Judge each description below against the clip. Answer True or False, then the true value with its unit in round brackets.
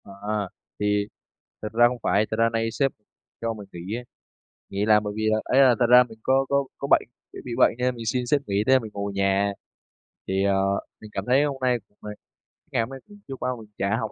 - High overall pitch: False (115 Hz)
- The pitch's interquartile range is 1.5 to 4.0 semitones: True (3.6 semitones)